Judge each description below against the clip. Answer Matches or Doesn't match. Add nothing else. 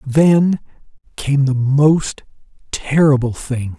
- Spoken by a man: Matches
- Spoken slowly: Matches